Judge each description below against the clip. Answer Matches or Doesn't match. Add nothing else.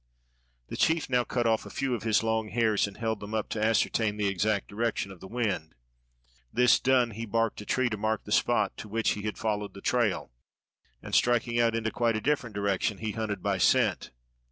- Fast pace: Matches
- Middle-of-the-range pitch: Doesn't match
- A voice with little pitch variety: Matches